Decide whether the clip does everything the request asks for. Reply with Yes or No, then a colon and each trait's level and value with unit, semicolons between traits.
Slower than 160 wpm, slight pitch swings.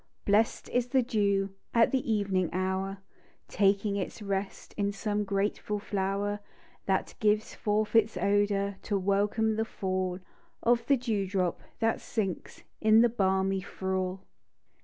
Yes: average, 140 wpm; narrow, 2.0 semitones